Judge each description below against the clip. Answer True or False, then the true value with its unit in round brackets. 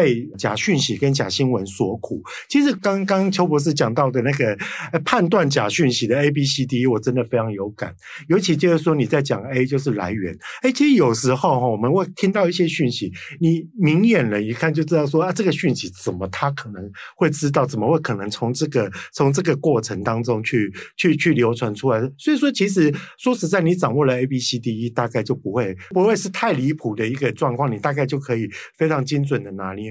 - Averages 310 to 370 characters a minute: True (325 characters per minute)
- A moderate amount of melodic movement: False (5.7 semitones)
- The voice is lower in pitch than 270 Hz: True (140 Hz)